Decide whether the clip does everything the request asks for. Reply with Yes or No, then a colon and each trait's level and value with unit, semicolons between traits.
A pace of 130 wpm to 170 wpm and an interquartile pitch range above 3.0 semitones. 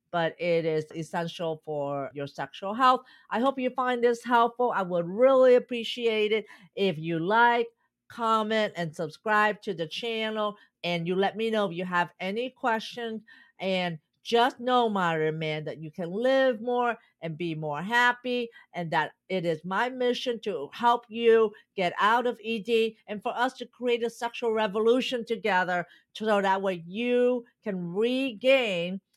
Yes: average, 165 wpm; wide, 5.4 semitones